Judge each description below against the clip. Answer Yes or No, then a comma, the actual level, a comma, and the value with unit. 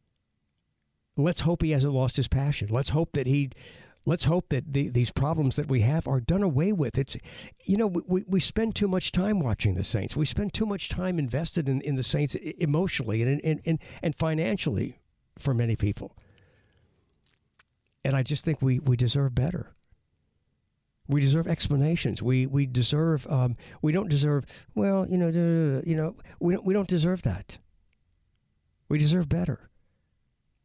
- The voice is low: No, medium, 145 Hz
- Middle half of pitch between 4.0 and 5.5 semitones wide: Yes, average, 5.0 semitones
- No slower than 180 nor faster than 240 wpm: No, average, 170 wpm